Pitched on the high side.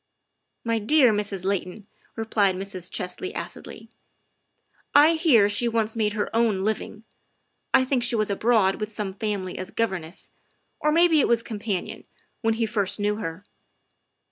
Yes: high, 215 Hz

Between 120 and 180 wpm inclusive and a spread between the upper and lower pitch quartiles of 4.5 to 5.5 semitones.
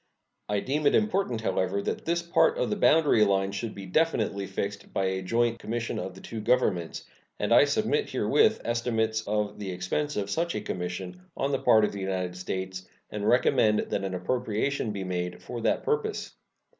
No: average, 190 wpm; average, 5.0 semitones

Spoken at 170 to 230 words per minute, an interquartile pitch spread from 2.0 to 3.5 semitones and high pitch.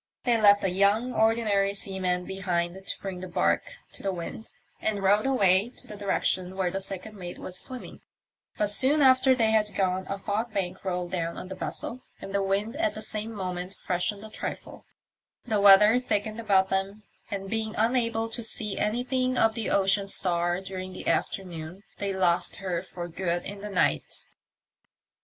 Yes: average, 180 wpm; average, 2.8 semitones; high, 200 Hz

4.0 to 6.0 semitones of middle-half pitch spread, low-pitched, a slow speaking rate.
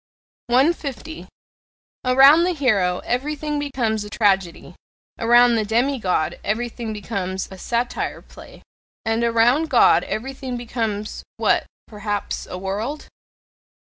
No: average, 4.4 semitones; high, 235 Hz; slow, 110 wpm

